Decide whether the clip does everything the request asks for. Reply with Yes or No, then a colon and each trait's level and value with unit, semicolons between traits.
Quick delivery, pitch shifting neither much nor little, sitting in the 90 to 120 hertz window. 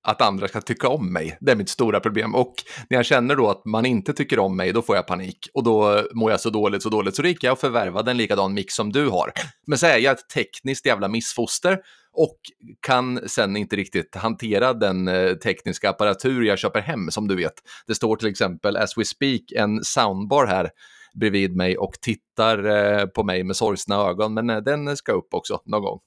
Yes: fast, 220 wpm; average, 3.7 semitones; low, 110 Hz